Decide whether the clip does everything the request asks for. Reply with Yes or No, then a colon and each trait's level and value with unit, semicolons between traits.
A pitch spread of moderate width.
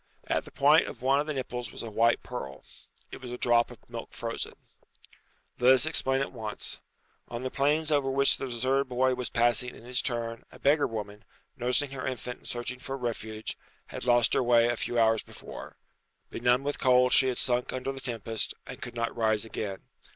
No: narrow, 2.2 semitones